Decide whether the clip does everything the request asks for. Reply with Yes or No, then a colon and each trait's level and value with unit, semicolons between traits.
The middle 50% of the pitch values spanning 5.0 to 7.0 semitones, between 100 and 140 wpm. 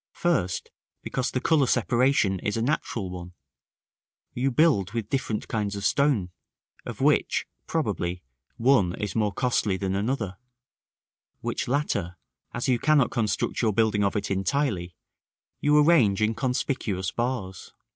Yes: average, 5.3 semitones; slow, 135 wpm